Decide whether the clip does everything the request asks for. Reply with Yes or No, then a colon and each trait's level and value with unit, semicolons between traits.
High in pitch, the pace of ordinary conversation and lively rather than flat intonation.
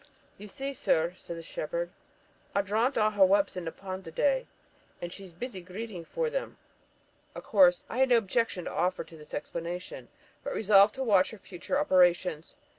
No: high, 195 Hz; average, 190 wpm; average, 4.6 semitones